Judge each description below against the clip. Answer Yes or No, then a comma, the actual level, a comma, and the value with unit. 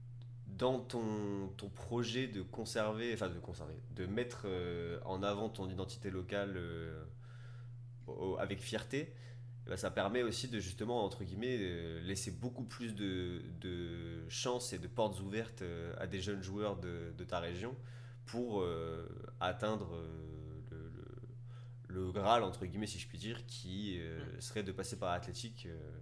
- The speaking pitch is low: Yes, low, 110 Hz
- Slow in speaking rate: Yes, slow, 140 wpm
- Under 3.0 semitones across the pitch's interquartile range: No, average, 4.2 semitones